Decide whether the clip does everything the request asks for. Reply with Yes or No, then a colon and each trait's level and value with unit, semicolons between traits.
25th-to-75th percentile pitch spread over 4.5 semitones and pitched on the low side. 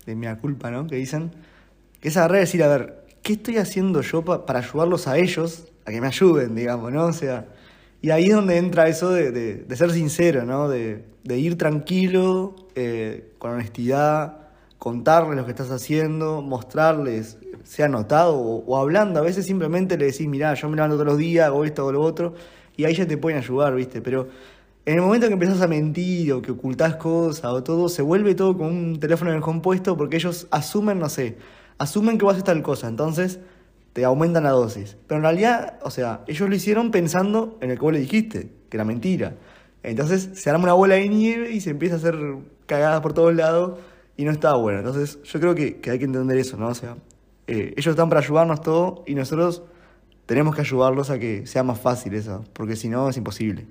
No: average, 5.1 semitones; medium, 155 Hz